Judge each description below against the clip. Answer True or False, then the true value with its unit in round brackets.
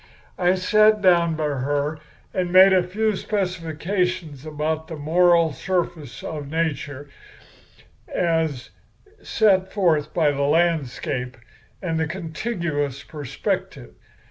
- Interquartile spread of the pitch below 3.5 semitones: False (3.8 semitones)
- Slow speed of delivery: True (110 wpm)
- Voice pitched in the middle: True (165 Hz)